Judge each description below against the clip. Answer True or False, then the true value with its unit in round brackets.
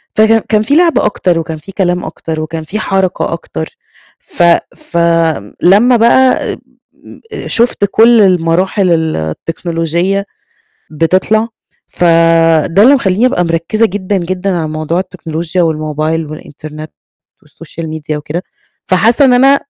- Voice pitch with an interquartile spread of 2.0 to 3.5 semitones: False (4.2 semitones)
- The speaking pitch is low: False (175 Hz)